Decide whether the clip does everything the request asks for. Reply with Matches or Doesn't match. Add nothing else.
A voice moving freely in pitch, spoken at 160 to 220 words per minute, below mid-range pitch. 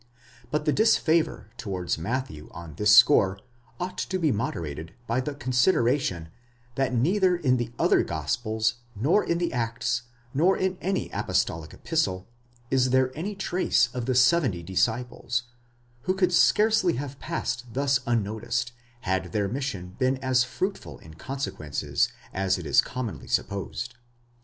Doesn't match